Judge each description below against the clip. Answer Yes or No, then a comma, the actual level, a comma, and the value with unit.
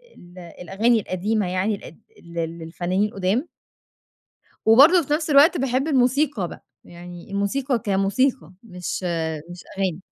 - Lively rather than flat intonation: Yes, wide, 6.4 semitones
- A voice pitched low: No, high, 200 Hz